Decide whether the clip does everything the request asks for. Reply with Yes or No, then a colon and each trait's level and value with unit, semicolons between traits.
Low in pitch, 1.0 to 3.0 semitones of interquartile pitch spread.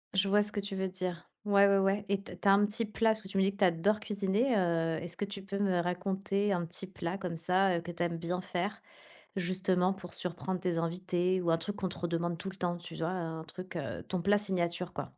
No: medium, 185 Hz; narrow, 2.4 semitones